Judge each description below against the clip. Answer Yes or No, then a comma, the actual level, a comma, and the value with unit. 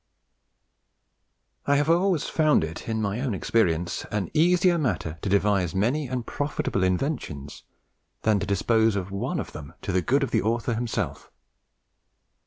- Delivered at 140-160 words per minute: Yes, average, 155 wpm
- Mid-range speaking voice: No, low, 110 Hz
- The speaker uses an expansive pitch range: Yes, wide, 7.0 semitones